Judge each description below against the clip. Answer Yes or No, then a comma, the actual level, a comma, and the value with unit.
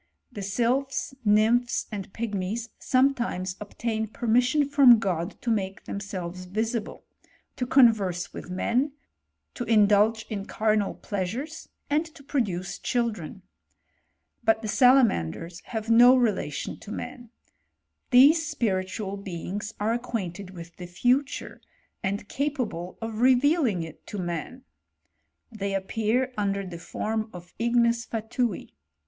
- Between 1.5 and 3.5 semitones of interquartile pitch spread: No, average, 4.2 semitones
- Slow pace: Yes, slow, 120 wpm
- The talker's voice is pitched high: Yes, high, 220 Hz